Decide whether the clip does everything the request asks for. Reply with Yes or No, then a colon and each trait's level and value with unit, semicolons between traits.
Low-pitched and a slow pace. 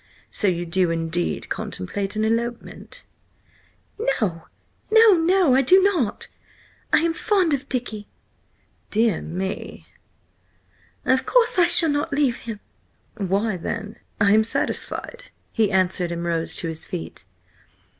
No: high, 220 Hz; slow, 130 wpm